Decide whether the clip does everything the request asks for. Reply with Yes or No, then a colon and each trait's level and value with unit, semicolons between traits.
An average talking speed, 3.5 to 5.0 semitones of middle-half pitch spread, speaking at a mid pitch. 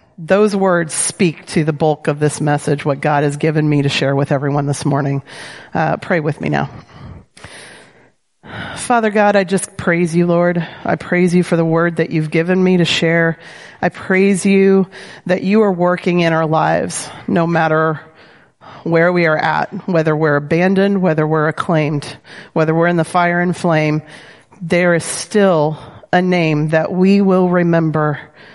No: average, 170 wpm; average, 3.0 semitones; medium, 170 Hz